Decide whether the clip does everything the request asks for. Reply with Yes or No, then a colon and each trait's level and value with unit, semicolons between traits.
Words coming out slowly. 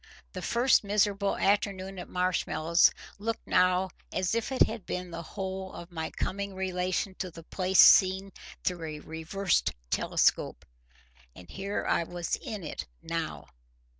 No: average, 145 wpm